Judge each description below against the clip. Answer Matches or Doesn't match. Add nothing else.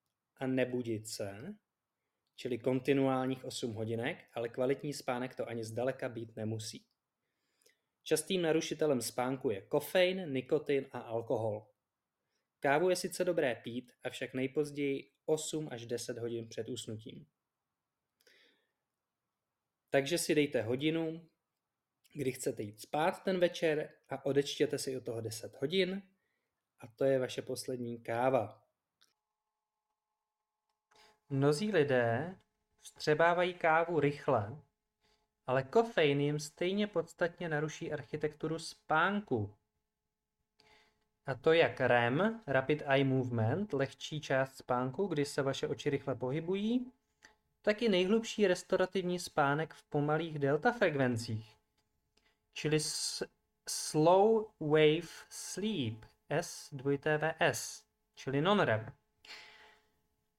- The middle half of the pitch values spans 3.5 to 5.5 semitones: Matches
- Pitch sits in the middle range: Matches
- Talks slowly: Matches